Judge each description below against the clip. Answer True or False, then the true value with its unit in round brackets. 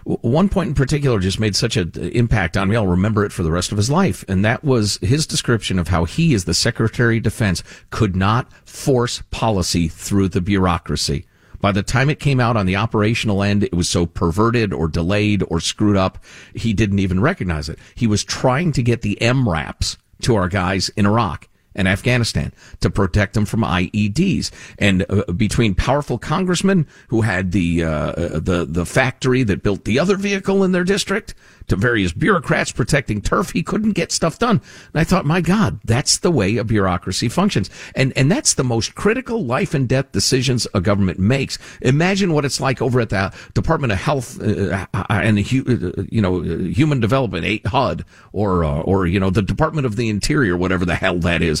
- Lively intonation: True (5.8 semitones)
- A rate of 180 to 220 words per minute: True (195 wpm)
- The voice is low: True (105 Hz)